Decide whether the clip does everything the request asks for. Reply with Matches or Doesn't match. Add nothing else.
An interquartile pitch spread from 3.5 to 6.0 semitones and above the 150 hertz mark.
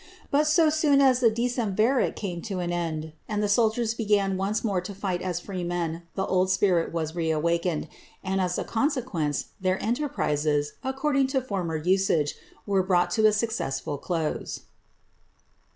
Matches